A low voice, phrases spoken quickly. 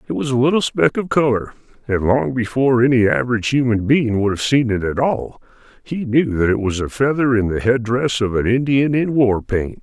Yes: low, 120 Hz; fast, 220 wpm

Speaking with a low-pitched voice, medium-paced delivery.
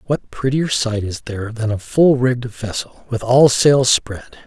Yes: low, 120 Hz; average, 190 wpm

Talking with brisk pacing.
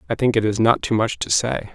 Yes: fast, 310 wpm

